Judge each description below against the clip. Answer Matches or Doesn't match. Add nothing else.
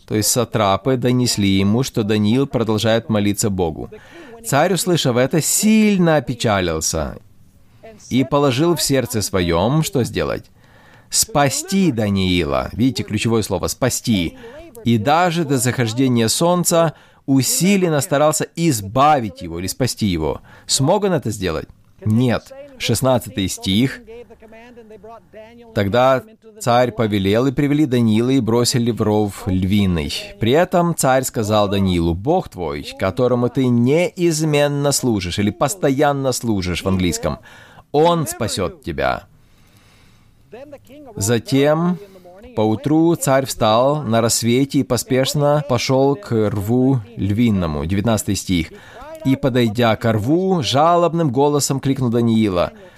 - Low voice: Matches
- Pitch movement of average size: Doesn't match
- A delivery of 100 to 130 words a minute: Matches